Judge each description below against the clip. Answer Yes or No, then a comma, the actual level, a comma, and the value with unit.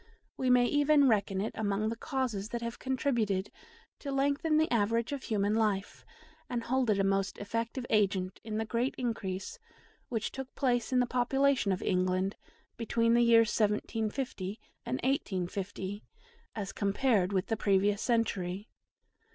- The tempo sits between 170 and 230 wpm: No, average, 150 wpm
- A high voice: Yes, high, 225 Hz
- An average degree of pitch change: Yes, average, 4.0 semitones